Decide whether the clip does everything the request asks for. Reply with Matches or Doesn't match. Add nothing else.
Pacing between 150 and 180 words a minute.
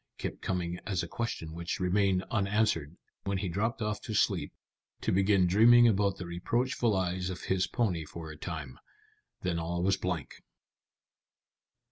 Matches